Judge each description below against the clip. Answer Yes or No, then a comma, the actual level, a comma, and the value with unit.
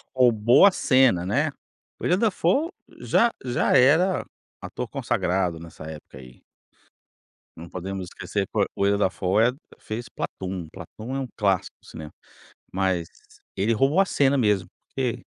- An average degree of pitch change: No, wide, 6.6 semitones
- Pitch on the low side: Yes, low, 105 Hz